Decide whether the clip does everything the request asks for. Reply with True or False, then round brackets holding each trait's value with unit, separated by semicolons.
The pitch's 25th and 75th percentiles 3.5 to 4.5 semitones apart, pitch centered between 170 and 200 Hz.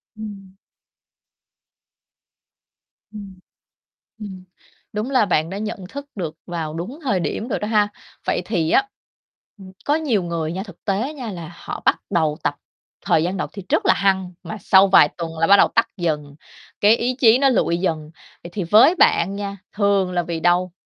True (3.8 semitones; 195 Hz)